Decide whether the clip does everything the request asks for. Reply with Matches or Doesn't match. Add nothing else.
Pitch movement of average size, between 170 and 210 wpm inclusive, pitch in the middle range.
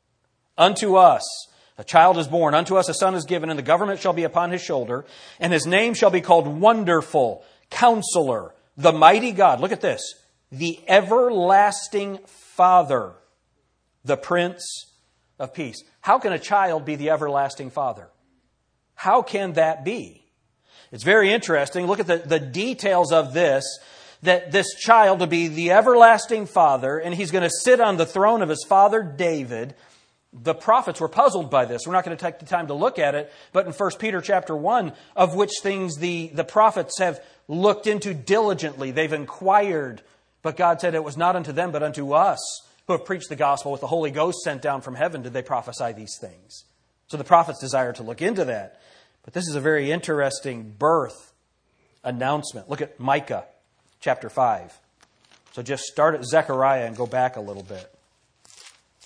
Matches